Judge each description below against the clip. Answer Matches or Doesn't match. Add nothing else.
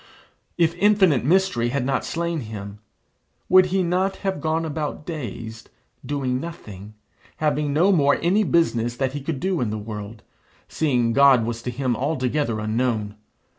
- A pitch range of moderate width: Doesn't match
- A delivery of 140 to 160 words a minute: Matches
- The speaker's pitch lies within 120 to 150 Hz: Matches